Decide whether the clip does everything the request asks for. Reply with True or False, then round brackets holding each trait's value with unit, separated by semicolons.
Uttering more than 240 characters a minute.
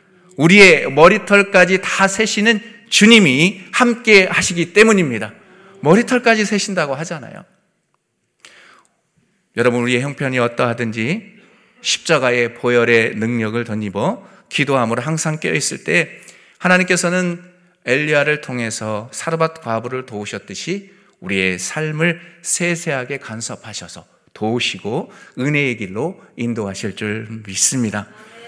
True (280 characters per minute)